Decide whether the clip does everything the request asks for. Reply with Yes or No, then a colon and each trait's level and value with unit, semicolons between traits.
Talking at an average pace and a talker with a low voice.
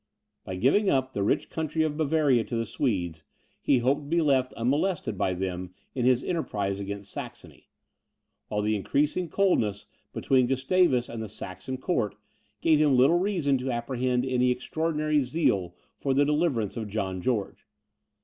Yes: average, 160 wpm; low, 130 Hz